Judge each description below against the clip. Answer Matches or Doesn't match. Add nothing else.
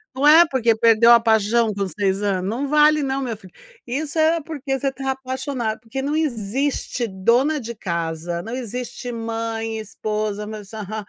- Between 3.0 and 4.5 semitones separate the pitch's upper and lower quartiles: Matches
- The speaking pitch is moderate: Doesn't match